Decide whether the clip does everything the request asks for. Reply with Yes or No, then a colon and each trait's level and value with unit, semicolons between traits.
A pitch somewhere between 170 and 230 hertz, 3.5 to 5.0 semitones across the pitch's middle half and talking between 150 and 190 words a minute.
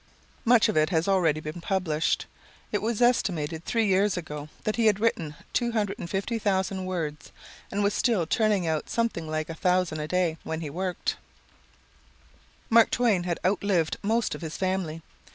Yes: medium, 185 Hz; average, 4.4 semitones; average, 160 wpm